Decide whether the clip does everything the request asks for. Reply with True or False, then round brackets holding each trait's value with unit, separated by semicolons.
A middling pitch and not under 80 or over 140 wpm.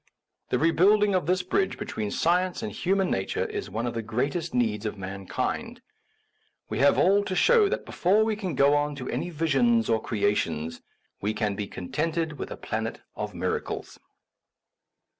False (145 Hz; 175 wpm)